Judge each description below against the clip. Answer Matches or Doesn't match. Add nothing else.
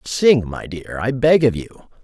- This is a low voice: Matches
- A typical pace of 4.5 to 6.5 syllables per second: Doesn't match